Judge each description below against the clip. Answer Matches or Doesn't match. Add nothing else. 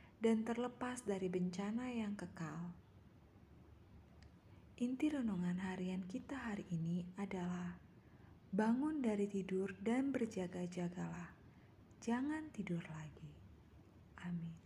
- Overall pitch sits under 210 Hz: Matches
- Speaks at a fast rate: Doesn't match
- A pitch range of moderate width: Matches